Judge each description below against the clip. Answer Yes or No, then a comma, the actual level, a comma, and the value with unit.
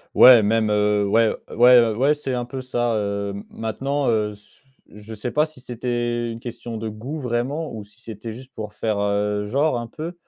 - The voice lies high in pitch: No, low, 115 Hz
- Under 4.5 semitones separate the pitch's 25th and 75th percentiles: Yes, average, 3.1 semitones